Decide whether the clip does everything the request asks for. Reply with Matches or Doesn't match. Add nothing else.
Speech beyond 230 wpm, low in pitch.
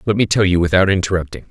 Matches